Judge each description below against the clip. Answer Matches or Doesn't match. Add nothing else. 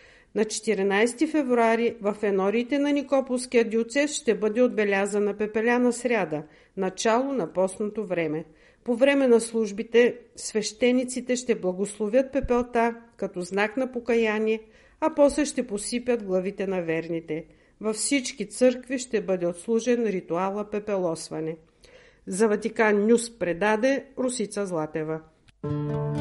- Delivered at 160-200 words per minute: Doesn't match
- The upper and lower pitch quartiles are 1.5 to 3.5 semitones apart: Doesn't match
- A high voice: Matches